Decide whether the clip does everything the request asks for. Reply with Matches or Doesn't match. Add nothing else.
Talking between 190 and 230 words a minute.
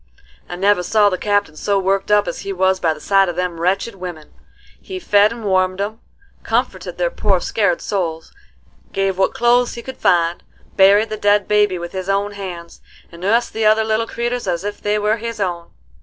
Matches